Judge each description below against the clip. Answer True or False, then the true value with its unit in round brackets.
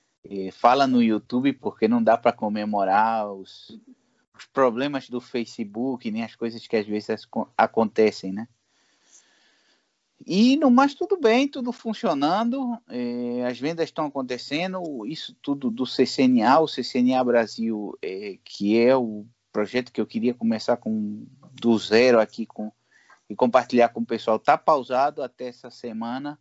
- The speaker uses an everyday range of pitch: False (6.1 semitones)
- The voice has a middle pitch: False (125 Hz)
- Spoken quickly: False (145 wpm)